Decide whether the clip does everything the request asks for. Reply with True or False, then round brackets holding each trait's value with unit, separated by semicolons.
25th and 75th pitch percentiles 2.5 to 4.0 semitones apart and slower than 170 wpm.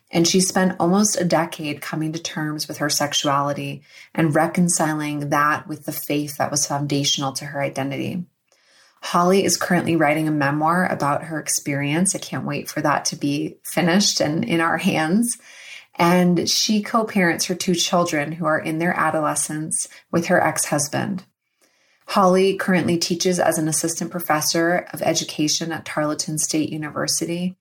True (2.9 semitones; 160 wpm)